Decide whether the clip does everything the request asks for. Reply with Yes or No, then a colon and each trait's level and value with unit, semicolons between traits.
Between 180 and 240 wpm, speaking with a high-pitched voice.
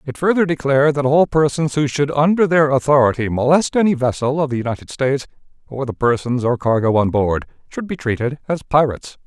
No: average, 195 wpm; medium, 140 Hz